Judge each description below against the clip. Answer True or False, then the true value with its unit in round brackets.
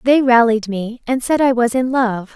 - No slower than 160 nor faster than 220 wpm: False (230 wpm)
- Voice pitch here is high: True (240 Hz)